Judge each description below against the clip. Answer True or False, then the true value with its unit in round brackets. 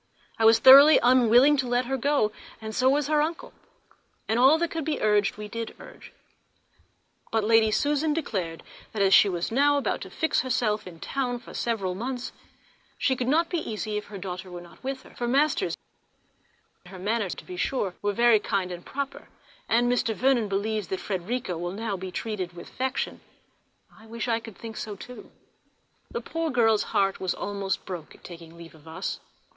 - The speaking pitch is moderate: False (225 Hz)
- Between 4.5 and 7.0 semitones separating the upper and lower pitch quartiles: True (5.1 semitones)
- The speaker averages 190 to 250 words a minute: True (195 wpm)